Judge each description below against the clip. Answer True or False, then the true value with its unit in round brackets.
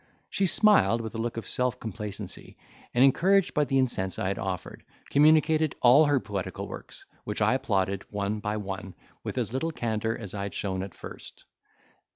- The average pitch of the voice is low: True (115 Hz)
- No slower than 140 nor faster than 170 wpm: False (185 wpm)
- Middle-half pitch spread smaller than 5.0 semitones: False (5.3 semitones)